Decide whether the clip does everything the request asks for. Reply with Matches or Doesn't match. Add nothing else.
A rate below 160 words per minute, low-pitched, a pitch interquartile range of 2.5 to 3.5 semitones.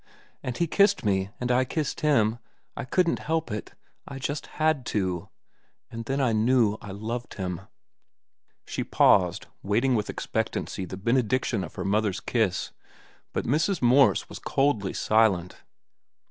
Doesn't match